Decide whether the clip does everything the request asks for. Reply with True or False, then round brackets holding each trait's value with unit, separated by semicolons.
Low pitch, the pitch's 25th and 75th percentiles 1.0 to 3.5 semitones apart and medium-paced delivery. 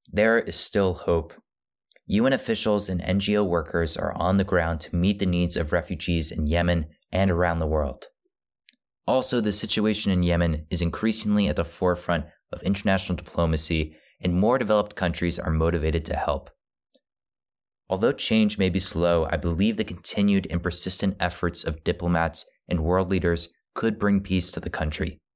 True (90 Hz; 2.9 semitones; 165 wpm)